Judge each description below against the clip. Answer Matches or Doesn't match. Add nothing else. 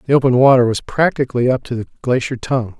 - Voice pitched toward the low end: Matches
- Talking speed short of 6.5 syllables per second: Doesn't match